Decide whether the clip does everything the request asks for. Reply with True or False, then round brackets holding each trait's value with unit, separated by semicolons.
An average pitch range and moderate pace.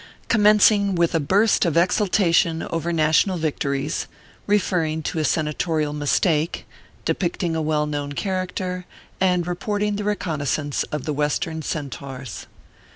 False (3.7 semitones; 130 wpm)